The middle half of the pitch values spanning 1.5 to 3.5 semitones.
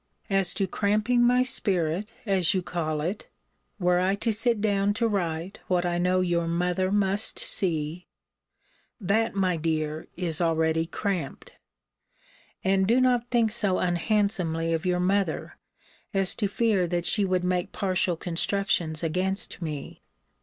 Yes: average, 3.0 semitones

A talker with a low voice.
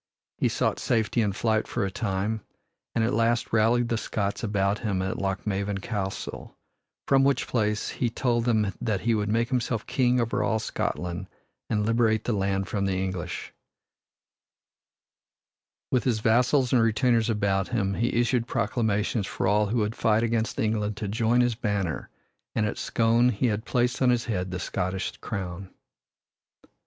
Yes: low, 110 Hz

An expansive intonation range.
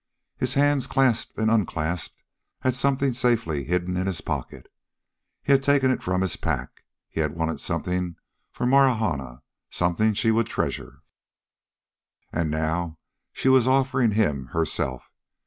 Yes: wide, 8.1 semitones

